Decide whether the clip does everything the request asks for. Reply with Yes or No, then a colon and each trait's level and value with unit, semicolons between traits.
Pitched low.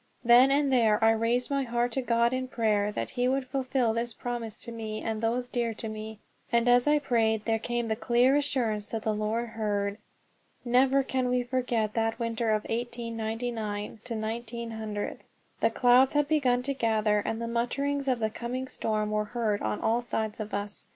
No: high, 235 Hz